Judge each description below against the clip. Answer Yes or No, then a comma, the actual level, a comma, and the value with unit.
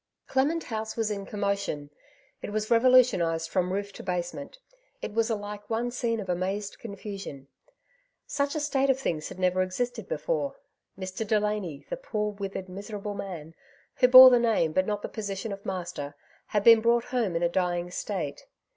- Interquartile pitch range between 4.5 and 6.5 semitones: No, average, 3.9 semitones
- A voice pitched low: No, high, 205 Hz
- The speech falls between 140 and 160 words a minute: No, average, 180 wpm